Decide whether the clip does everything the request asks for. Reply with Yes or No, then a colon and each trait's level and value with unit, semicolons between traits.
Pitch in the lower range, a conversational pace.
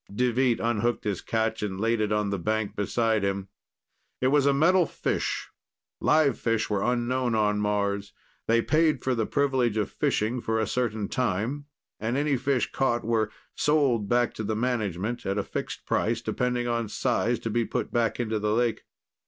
Yes: low, 115 Hz; average, 180 wpm